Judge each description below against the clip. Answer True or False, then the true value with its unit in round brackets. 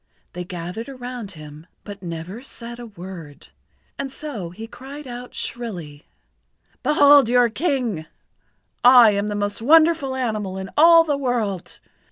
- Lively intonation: True (6.1 semitones)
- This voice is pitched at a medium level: False (225 Hz)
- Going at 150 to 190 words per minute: False (140 wpm)